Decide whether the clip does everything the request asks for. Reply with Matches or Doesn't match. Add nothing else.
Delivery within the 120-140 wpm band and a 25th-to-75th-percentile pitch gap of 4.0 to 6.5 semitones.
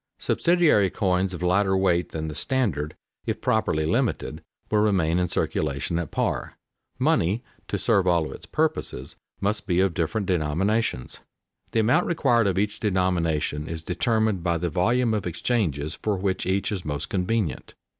Doesn't match